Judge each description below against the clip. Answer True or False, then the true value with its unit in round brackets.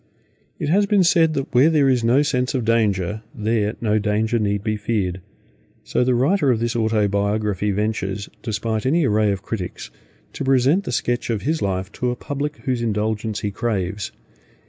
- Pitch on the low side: True (110 Hz)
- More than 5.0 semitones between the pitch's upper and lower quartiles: False (3.9 semitones)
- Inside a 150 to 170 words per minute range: False (180 wpm)